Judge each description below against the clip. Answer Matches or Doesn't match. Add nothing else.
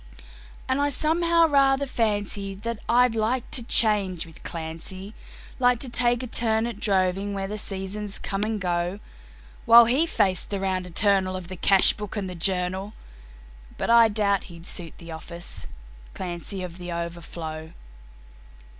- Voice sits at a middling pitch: Doesn't match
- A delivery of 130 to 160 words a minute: Matches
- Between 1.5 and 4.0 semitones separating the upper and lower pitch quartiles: Doesn't match